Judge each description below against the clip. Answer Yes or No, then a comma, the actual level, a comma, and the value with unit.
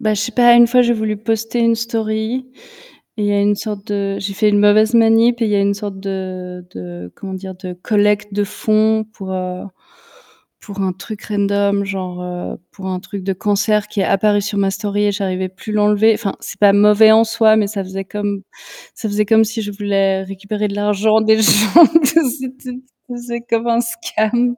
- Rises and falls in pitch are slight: Yes, narrow, 2.0 semitones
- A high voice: Yes, high, 210 Hz